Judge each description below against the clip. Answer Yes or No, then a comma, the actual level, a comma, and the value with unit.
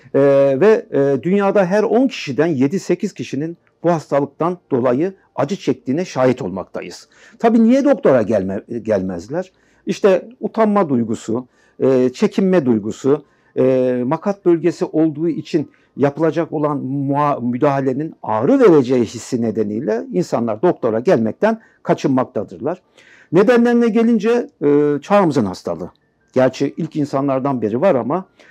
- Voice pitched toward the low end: No, medium, 150 Hz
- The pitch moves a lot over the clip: Yes, wide, 7.1 semitones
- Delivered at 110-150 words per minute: No, average, 100 wpm